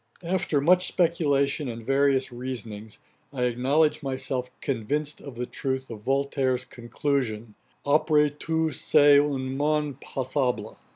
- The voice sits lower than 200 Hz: Yes, low, 135 Hz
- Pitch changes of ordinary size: Yes, average, 3.0 semitones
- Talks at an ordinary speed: No, slow, 125 wpm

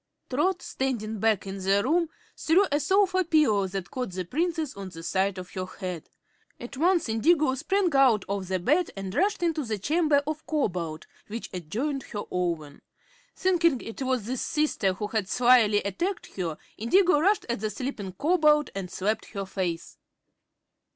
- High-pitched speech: Yes, high, 235 Hz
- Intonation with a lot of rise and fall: Yes, wide, 8.1 semitones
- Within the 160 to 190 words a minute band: Yes, average, 165 wpm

